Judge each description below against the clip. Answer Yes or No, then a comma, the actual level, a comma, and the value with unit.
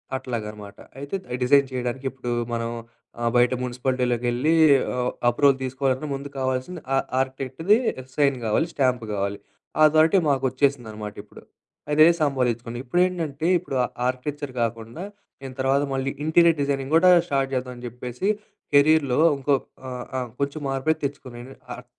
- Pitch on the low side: Yes, low, 130 Hz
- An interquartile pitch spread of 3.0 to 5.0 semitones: No, narrow, 2.6 semitones